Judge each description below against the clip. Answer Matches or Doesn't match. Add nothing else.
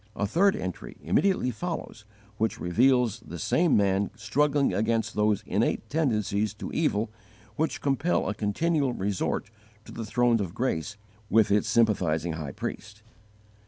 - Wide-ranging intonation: Doesn't match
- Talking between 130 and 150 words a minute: Matches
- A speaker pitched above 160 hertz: Doesn't match